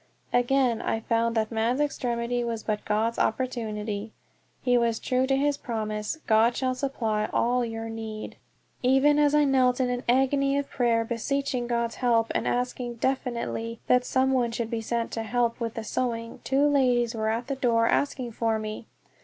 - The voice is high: Yes, high, 235 Hz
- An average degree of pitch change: No, narrow, 2.2 semitones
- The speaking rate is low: No, average, 185 wpm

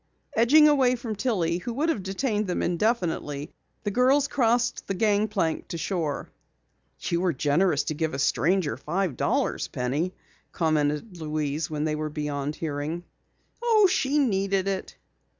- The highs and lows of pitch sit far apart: Yes, wide, 6.9 semitones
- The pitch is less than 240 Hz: Yes, medium, 185 Hz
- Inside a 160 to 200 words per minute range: No, average, 150 wpm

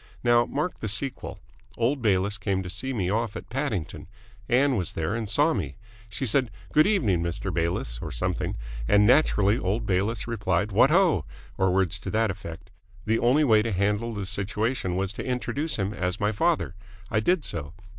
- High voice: No, low, 105 Hz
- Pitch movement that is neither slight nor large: Yes, average, 4.7 semitones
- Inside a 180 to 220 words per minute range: Yes, average, 185 wpm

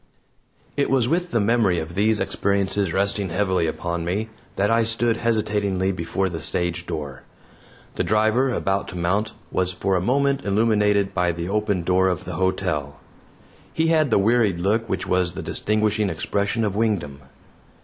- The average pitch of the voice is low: Yes, low, 100 Hz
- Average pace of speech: Yes, average, 165 wpm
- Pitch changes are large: No, average, 3.6 semitones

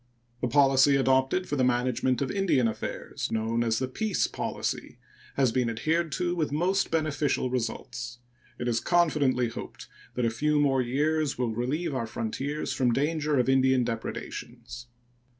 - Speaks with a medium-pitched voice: No, low, 130 Hz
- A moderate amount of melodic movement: Yes, average, 3.8 semitones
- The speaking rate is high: No, average, 155 wpm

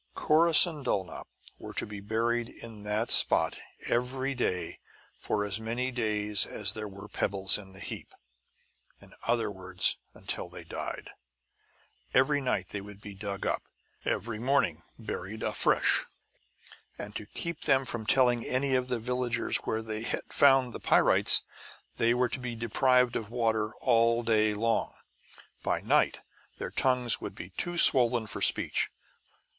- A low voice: Yes, low, 115 Hz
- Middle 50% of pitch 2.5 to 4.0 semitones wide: Yes, average, 3.3 semitones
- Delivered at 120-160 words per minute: Yes, average, 155 wpm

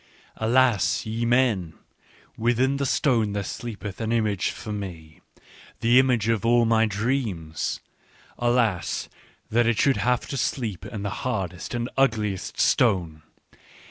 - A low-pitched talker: Yes, low, 110 Hz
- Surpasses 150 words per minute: No, average, 140 wpm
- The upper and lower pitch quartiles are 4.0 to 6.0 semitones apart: No, average, 3.4 semitones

